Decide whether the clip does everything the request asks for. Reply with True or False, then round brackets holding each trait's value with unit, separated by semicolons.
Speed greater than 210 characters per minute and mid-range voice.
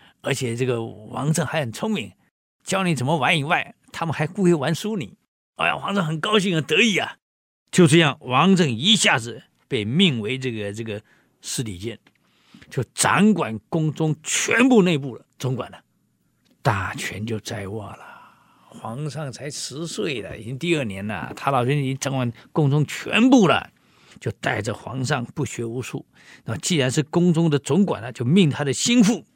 True (260 characters per minute; 150 Hz)